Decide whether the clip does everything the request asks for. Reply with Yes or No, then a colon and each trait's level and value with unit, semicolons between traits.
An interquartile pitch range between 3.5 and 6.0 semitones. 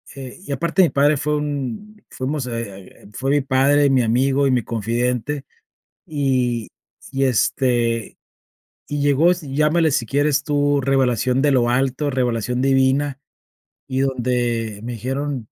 No: average, 2.8 semitones